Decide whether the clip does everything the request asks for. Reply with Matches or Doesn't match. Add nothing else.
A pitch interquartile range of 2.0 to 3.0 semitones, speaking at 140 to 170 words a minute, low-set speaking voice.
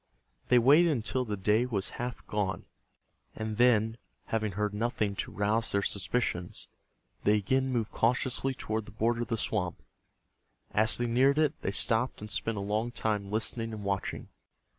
Matches